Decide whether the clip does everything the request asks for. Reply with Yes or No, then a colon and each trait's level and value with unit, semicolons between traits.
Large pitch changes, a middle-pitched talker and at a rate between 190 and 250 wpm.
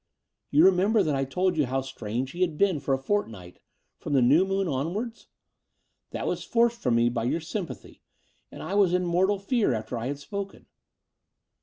Yes: wide, 6.7 semitones; medium, 165 Hz; average, 195 wpm